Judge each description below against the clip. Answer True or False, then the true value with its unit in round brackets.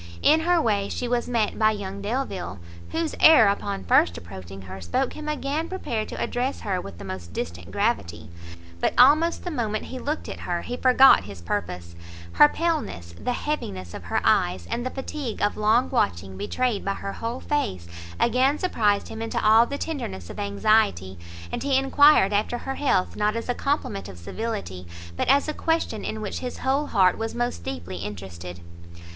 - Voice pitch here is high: True (215 Hz)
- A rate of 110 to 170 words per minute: False (185 wpm)